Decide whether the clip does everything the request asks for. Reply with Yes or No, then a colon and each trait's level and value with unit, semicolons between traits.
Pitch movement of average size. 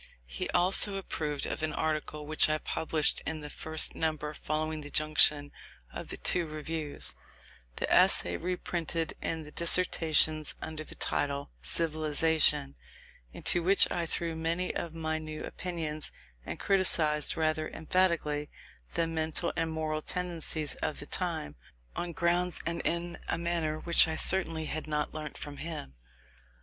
No: narrow, 1.8 semitones